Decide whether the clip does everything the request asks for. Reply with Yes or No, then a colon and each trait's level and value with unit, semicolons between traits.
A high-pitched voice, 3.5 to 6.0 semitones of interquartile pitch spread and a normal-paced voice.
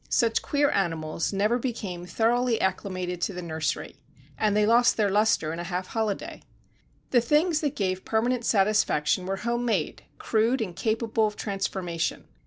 Yes: high, 210 Hz; average, 4.2 semitones; average, 160 wpm